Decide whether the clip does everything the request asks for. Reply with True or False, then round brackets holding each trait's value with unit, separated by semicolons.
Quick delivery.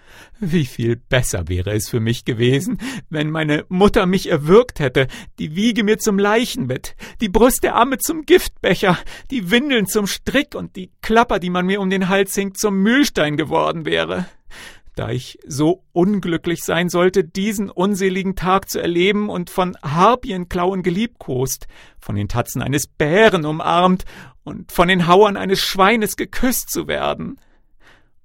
False (155 wpm)